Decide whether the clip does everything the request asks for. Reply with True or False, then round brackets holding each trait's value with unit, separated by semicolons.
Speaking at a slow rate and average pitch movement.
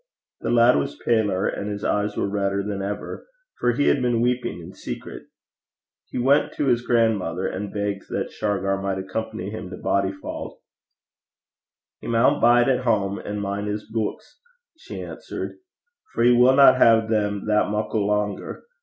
False (165 wpm; 3.2 semitones)